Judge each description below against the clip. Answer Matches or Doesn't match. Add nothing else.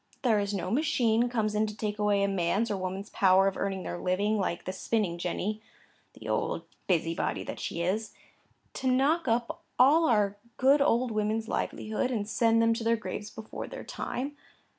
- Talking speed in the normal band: Matches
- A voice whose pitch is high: Matches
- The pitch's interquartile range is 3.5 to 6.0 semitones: Doesn't match